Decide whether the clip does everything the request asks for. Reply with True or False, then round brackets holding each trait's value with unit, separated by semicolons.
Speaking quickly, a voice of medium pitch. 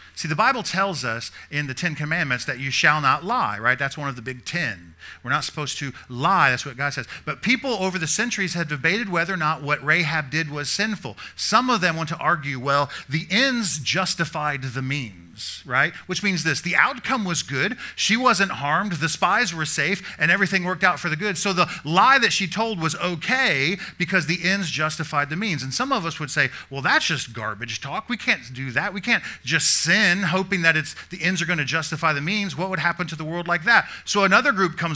True (230 wpm; 165 Hz)